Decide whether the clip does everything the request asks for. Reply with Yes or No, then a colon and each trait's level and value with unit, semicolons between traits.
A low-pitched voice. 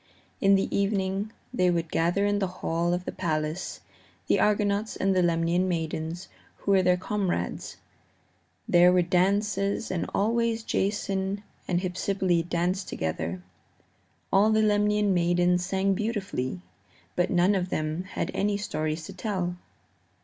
No: medium, 185 Hz